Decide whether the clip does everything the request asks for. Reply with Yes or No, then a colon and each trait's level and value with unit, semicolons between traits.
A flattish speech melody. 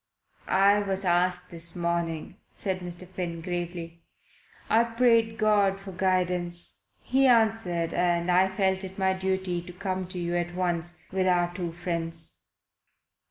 Yes: narrow, 1.7 semitones